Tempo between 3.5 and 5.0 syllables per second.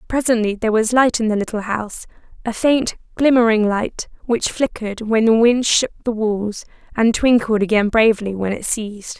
No: 5.2 syllables/s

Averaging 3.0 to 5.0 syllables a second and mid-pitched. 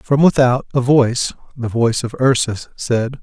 No: 4.6 syllables/s; low, 125 Hz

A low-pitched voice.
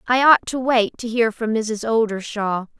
No: high, 225 Hz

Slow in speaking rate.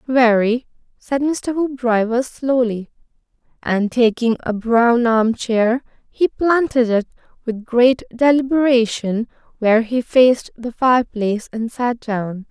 Yes: slow, 115 wpm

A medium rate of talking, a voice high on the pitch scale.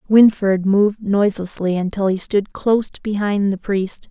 Yes: average, 145 wpm; high, 200 Hz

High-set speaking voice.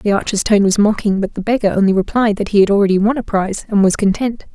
Yes: high, 205 Hz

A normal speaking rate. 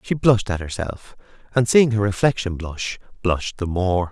Yes: average, 175 wpm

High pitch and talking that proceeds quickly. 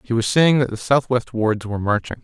No: low, 120 Hz; fast, 240 wpm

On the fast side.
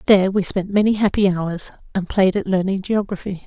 No: average, 190 wpm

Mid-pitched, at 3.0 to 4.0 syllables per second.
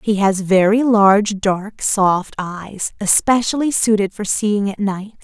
No: high, 205 Hz; 3.9 syllables/s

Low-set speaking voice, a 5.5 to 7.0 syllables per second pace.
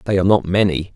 No: very low, 95 Hz; 7.4 syllables/s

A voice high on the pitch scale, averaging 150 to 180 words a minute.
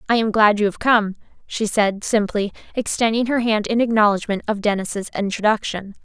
Yes: high, 210 Hz; average, 170 wpm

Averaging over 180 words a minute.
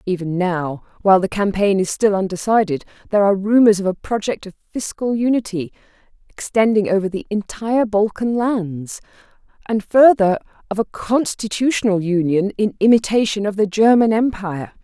No: average, 140 wpm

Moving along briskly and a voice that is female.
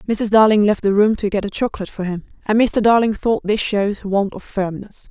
Yes: fast, 235 wpm; female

